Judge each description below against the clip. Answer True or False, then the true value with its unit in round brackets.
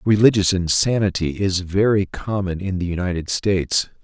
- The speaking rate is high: False (135 wpm)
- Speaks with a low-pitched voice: True (95 Hz)